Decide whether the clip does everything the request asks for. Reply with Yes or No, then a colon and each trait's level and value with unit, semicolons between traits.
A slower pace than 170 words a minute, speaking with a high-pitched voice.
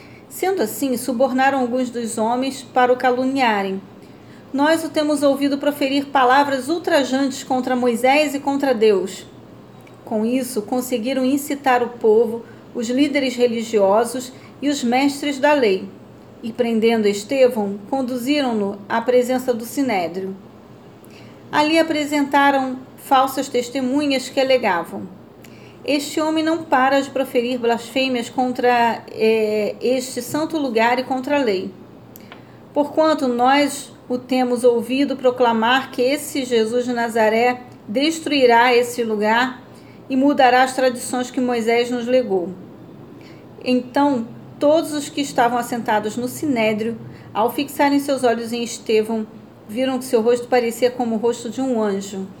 Yes: average, 130 wpm; very high, 255 Hz